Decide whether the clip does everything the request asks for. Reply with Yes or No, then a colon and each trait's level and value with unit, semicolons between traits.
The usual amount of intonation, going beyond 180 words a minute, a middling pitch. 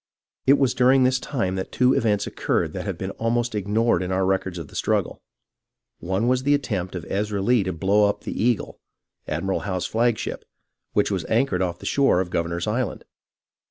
No: average, 4.7 semitones; average, 195 wpm; low, 105 Hz